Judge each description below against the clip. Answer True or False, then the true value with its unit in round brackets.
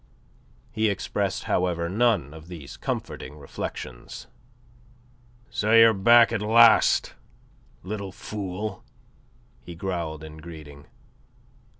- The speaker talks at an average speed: False (95 wpm)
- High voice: False (90 Hz)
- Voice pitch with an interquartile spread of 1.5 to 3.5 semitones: False (5.4 semitones)